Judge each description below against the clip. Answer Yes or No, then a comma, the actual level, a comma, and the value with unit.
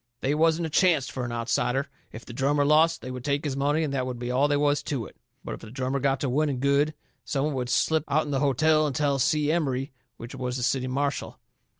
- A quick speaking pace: Yes, fast, 250 wpm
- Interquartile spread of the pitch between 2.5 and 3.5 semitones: Yes, average, 2.8 semitones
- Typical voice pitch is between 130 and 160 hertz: Yes, medium, 140 Hz